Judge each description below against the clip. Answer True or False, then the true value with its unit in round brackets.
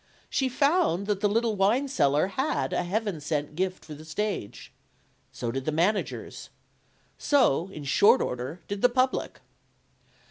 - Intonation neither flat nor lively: False (7.3 semitones)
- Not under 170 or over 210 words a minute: False (150 wpm)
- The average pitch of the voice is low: False (195 Hz)